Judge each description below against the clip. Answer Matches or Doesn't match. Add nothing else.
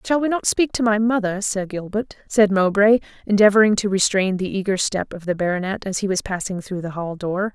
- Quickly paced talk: Matches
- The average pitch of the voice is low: Doesn't match